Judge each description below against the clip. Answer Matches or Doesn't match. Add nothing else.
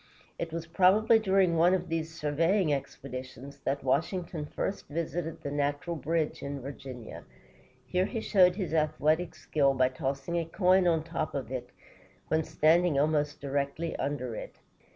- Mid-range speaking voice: Matches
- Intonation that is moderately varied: Matches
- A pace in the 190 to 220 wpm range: Doesn't match